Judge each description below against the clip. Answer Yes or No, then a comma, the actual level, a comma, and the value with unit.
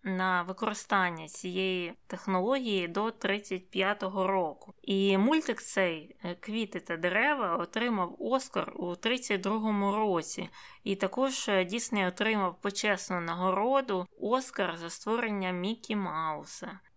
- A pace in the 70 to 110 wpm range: Yes, slow, 105 wpm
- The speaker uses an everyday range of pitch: Yes, average, 3.2 semitones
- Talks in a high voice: Yes, high, 195 Hz